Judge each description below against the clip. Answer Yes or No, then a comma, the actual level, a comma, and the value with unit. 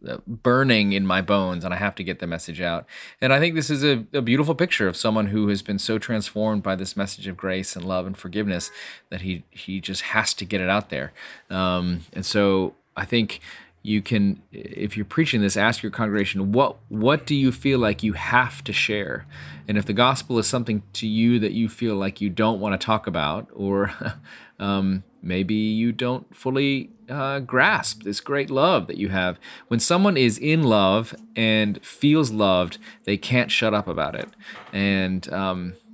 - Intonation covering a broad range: No, average, 3.9 semitones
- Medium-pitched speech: No, low, 105 Hz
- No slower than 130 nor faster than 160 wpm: No, average, 200 wpm